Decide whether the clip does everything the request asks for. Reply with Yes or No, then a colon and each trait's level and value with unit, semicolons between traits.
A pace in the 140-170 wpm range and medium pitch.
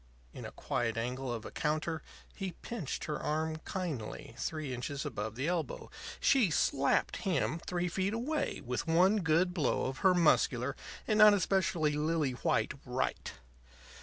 Yes: average, 155 wpm; medium, 160 Hz